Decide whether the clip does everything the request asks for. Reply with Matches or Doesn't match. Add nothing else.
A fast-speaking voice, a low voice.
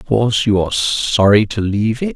Doesn't match